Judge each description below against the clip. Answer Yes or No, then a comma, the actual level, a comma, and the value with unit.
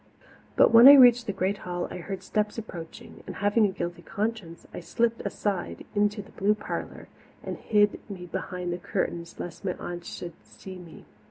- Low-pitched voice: No, high, 195 Hz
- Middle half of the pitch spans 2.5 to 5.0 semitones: Yes, average, 3.3 semitones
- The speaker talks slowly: No, average, 185 wpm